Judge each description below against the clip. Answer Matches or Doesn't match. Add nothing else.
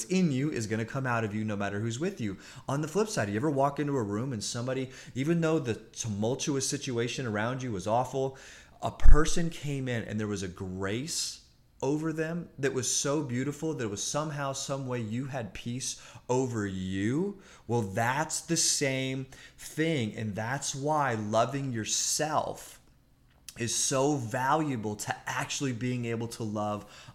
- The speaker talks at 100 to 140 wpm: Doesn't match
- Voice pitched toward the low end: Matches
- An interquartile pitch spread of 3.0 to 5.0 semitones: Matches